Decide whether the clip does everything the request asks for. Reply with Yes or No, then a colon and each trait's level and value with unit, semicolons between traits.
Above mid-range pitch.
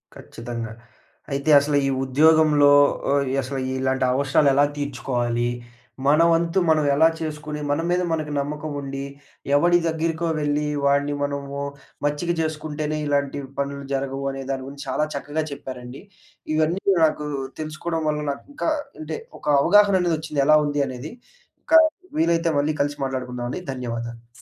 No: medium, 145 Hz